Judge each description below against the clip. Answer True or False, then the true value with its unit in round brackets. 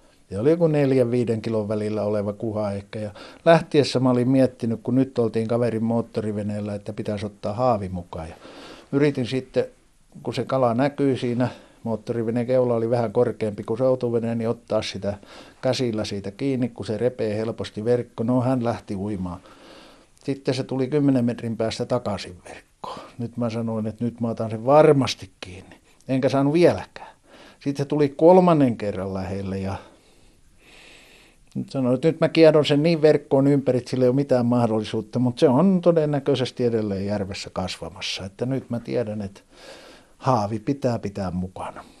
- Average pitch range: True (3.7 semitones)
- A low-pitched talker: True (120 Hz)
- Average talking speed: False (165 wpm)